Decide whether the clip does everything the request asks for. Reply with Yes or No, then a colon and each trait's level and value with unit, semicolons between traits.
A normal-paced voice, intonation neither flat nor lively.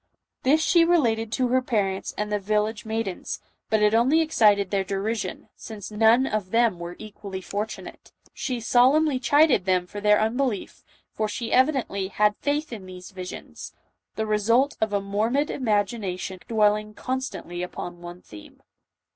Yes: average, 155 wpm; average, 3.9 semitones